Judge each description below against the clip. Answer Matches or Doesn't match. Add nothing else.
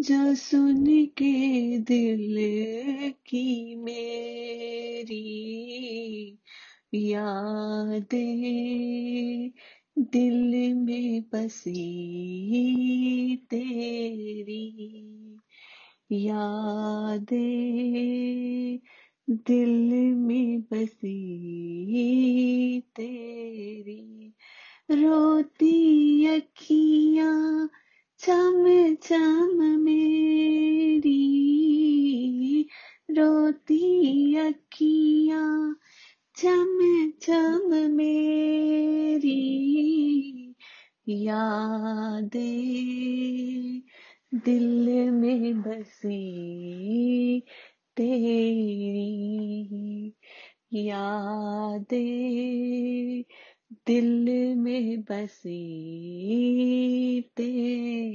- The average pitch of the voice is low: Doesn't match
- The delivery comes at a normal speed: Doesn't match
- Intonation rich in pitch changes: Doesn't match